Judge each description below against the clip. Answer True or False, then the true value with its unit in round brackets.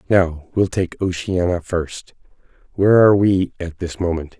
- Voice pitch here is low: True (90 Hz)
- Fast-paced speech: False (150 wpm)